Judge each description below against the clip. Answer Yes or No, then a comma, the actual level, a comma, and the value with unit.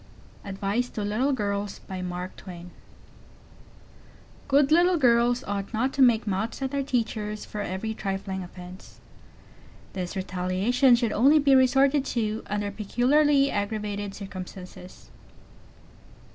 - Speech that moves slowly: Yes, slow, 110 wpm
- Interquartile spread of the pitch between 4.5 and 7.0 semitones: Yes, average, 4.9 semitones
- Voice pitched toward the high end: Yes, high, 210 Hz